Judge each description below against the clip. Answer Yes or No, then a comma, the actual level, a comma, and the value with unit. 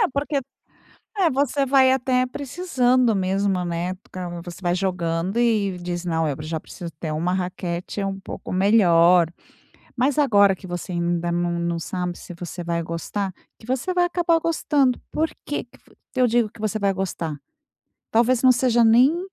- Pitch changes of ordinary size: No, wide, 6.5 semitones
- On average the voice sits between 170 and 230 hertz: Yes, high, 195 Hz